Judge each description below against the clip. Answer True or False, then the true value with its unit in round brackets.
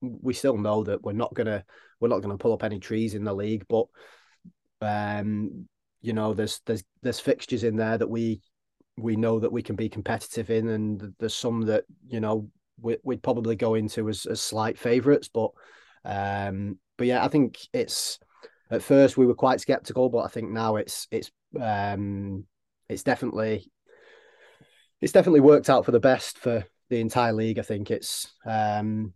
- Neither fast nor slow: True (185 wpm)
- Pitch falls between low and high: False (110 Hz)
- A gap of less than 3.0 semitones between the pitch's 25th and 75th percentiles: True (2.4 semitones)